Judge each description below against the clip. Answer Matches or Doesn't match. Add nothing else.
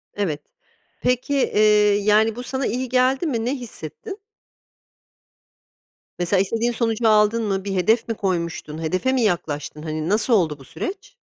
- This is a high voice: Matches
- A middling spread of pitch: Doesn't match